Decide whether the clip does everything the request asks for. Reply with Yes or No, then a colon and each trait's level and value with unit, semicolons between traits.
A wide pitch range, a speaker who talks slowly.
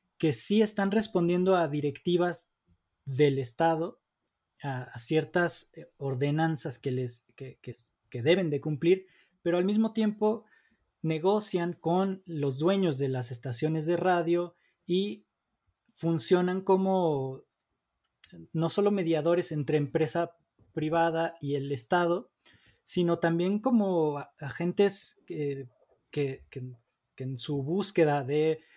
No: average, 4.1 semitones; slow, 120 wpm